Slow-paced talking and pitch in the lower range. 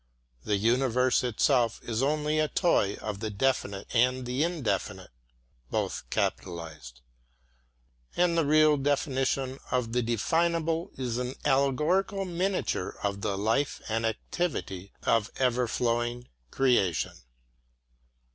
Yes: slow, 110 wpm; low, 125 Hz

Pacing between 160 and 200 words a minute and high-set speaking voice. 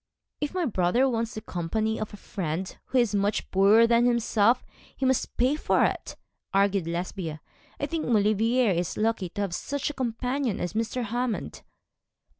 Yes: average, 170 wpm; high, 220 Hz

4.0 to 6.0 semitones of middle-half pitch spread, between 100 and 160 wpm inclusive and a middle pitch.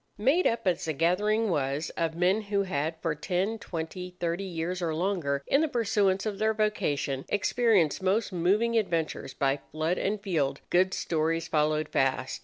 No: average, 4.5 semitones; average, 170 wpm; medium, 180 Hz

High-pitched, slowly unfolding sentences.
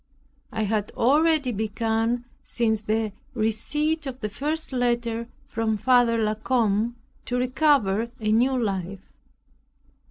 Yes: high, 230 Hz; slow, 120 wpm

